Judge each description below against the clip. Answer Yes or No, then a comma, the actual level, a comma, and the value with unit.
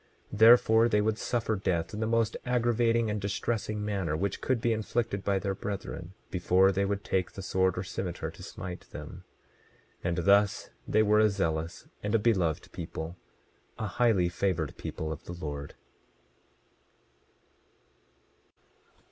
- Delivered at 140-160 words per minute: Yes, average, 150 wpm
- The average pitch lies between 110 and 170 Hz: No, low, 100 Hz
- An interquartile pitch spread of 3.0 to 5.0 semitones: Yes, average, 3.6 semitones